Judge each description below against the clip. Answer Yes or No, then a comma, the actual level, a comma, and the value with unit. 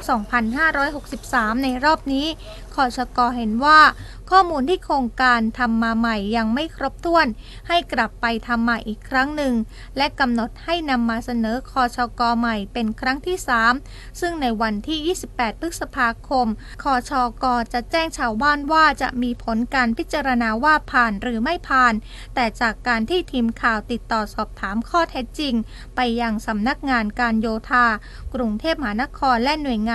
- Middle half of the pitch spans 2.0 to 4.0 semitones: Yes, average, 3.7 semitones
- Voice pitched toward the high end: Yes, very high, 250 Hz